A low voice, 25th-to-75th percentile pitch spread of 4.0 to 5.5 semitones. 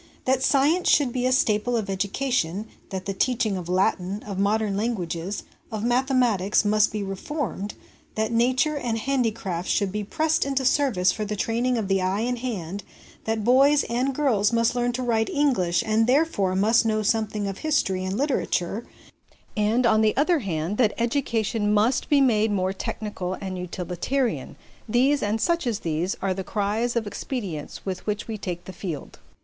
No: high, 220 Hz; average, 4.3 semitones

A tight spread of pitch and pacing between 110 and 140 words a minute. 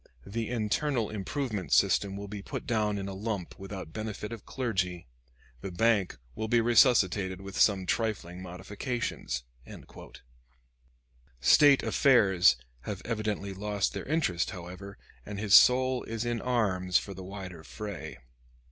No: average, 3.4 semitones; slow, 135 wpm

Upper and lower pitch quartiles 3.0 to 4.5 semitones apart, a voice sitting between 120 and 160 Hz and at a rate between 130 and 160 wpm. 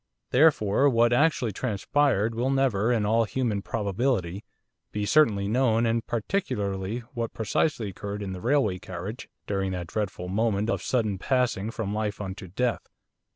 No: average, 3.8 semitones; low, 110 Hz; average, 150 wpm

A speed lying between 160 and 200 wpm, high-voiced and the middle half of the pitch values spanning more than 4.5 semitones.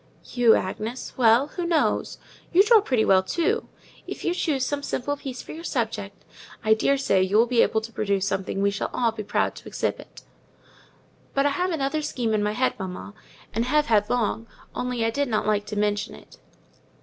Yes: average, 195 wpm; high, 235 Hz; average, 5.3 semitones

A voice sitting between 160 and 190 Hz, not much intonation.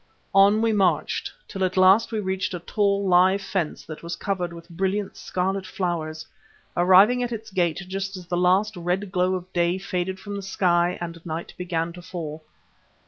Yes: medium, 185 Hz; narrow, 2.1 semitones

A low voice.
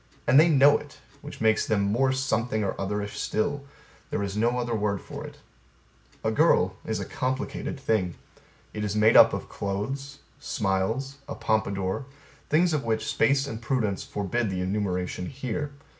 Yes: low, 110 Hz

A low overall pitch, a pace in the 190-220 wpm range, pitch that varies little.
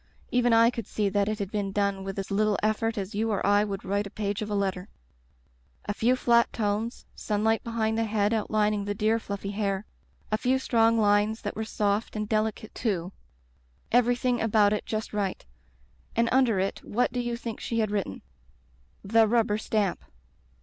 No: high, 215 Hz; average, 200 wpm; narrow, 2.0 semitones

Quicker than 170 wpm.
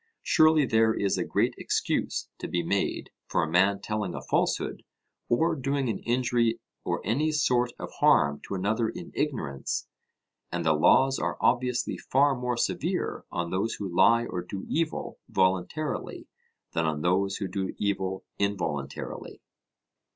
No: average, 150 wpm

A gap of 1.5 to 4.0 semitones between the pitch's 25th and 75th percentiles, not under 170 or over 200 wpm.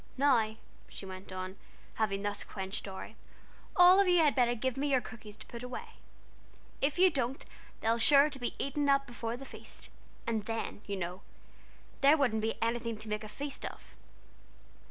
No: average, 4.6 semitones; average, 185 wpm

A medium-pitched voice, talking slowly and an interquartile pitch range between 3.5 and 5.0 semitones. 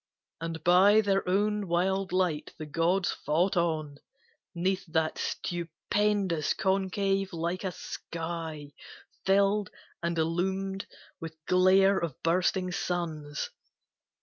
No: medium, 180 Hz; slow, 105 wpm; average, 2.8 semitones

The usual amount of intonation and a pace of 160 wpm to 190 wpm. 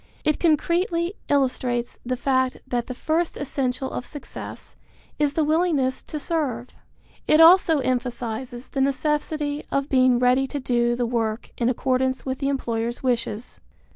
No: average, 3.4 semitones; average, 145 wpm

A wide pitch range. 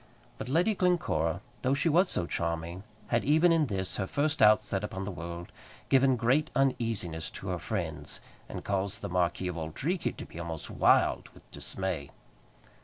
Yes: wide, 8.7 semitones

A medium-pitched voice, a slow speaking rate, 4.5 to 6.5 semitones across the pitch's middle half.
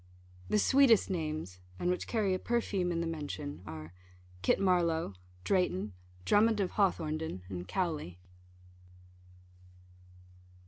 Yes: medium, 170 Hz; slow, 110 wpm; average, 5.3 semitones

